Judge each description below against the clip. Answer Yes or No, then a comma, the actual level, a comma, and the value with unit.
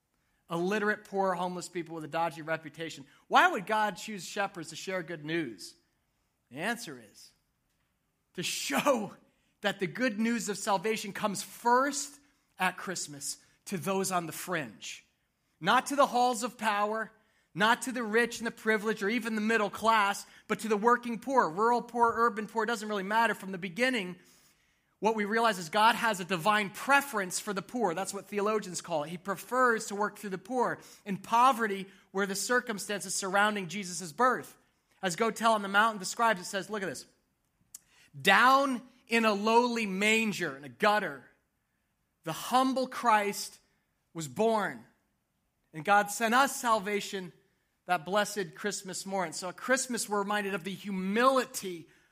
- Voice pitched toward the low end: No, high, 210 Hz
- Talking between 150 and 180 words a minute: Yes, average, 165 wpm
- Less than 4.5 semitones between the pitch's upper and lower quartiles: Yes, average, 3.3 semitones